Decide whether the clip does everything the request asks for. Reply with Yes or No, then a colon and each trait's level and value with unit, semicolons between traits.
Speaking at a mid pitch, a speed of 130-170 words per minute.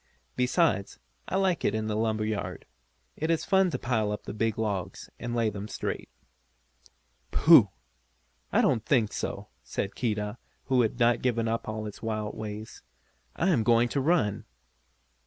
No: low, 110 Hz; average, 165 wpm